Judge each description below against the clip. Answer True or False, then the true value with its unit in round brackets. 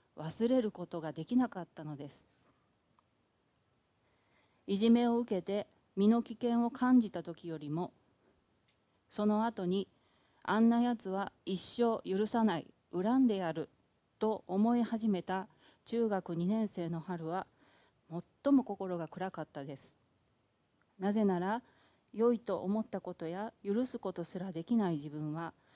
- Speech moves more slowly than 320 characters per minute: True (245 characters per minute)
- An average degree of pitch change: True (4.9 semitones)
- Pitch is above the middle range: True (195 Hz)